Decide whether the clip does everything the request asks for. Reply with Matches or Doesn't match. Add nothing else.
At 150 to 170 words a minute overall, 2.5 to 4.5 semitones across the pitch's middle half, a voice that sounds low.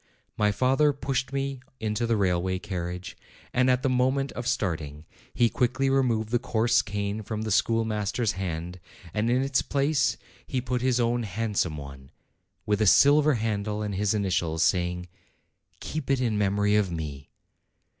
Doesn't match